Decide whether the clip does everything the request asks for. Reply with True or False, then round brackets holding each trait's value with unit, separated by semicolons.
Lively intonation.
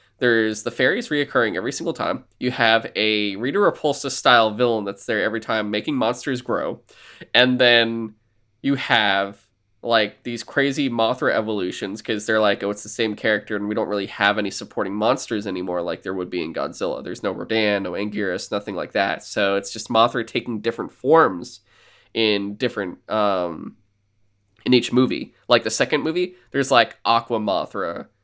False (2.8 semitones)